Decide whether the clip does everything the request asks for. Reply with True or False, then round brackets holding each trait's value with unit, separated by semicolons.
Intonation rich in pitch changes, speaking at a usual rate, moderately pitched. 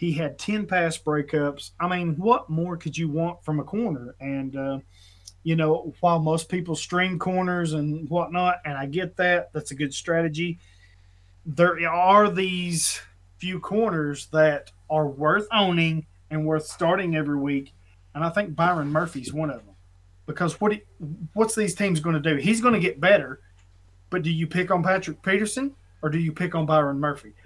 False (3.9 semitones; 185 wpm; 160 Hz)